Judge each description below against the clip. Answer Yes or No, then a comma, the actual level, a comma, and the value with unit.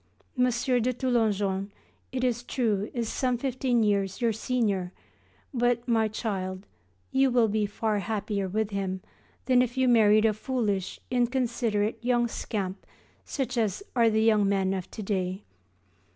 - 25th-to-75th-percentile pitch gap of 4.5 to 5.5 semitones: No, average, 3.3 semitones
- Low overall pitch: No, high, 220 Hz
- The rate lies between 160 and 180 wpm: No, average, 150 wpm